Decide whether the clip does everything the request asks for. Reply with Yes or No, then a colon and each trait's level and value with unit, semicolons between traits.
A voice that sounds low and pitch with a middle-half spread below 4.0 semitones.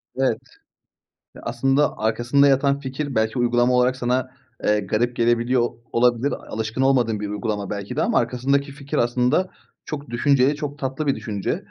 Yes: low, 125 Hz; average, 2.9 semitones